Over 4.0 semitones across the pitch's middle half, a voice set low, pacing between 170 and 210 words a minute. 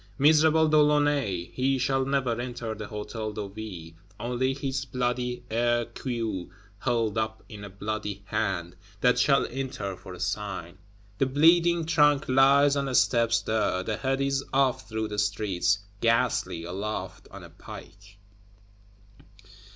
No: average, 4.8 semitones; low, 115 Hz; average, 145 wpm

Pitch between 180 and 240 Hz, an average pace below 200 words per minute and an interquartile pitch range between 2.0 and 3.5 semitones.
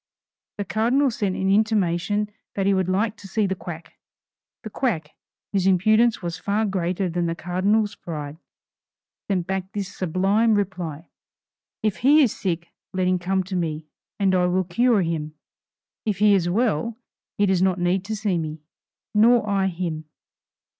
Yes: high, 190 Hz; average, 165 wpm; average, 3.2 semitones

